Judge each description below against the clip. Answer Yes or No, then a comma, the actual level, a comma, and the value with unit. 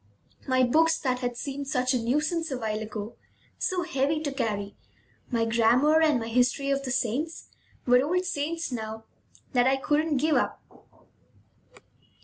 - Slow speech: No, average, 155 wpm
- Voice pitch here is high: Yes, very high, 265 Hz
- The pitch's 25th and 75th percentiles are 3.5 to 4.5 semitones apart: Yes, average, 4.2 semitones